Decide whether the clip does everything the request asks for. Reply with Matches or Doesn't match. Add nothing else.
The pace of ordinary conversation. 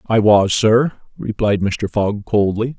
Matches